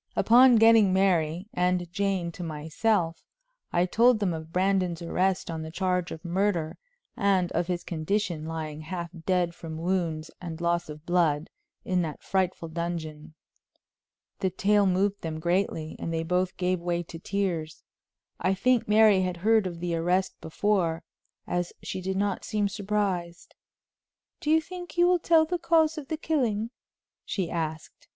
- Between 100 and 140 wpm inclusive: No, average, 160 wpm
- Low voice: No, medium, 180 Hz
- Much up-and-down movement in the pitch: No, average, 3.4 semitones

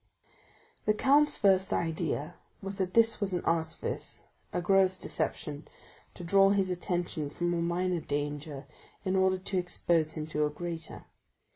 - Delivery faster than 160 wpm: No, average, 150 wpm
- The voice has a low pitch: No, medium, 175 Hz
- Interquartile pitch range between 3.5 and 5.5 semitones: No, average, 3.1 semitones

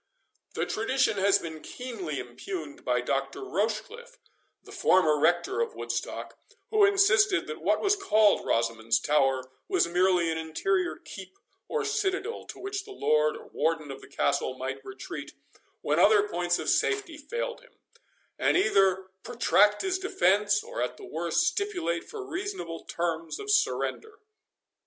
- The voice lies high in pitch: Yes, high, 225 Hz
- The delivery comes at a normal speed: Yes, average, 150 wpm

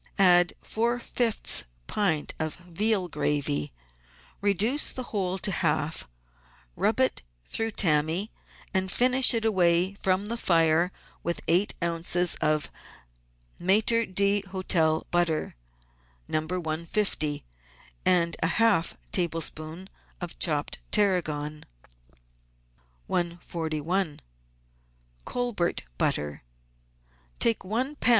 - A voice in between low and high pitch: Yes, medium, 180 Hz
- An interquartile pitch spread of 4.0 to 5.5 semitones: Yes, average, 4.3 semitones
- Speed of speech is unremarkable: No, slow, 100 wpm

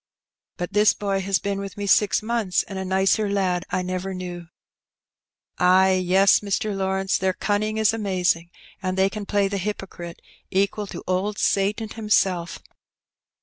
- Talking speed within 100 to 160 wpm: Yes, average, 155 wpm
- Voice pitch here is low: No, high, 195 Hz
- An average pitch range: No, narrow, 1.8 semitones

